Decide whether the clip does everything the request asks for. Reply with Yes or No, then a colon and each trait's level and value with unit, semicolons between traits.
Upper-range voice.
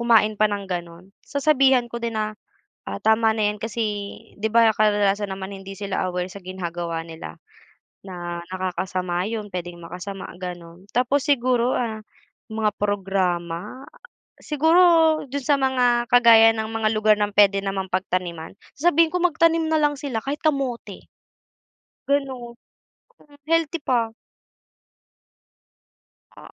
Yes: high, 215 Hz